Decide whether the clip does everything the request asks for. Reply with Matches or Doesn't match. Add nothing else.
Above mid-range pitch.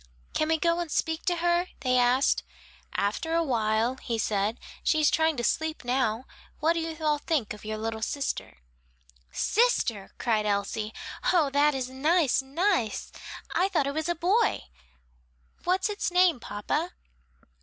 Matches